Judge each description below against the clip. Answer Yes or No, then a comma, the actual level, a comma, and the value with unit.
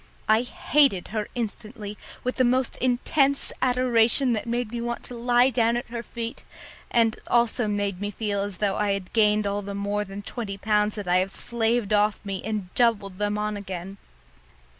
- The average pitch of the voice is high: Yes, high, 215 Hz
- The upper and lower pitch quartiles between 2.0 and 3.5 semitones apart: Yes, average, 2.8 semitones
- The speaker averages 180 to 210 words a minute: Yes, average, 185 wpm